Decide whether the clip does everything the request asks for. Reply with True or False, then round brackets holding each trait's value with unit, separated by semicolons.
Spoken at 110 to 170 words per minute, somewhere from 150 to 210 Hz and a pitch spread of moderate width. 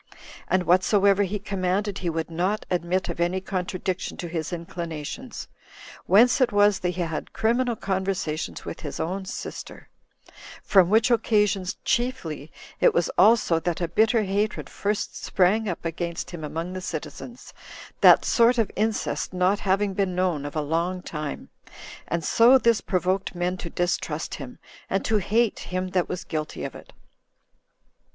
True (160 wpm; 185 Hz; 3.3 semitones)